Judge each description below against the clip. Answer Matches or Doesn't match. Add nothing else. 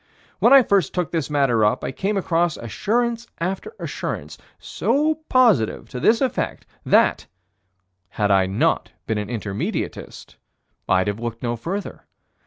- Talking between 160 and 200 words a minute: Doesn't match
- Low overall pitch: Doesn't match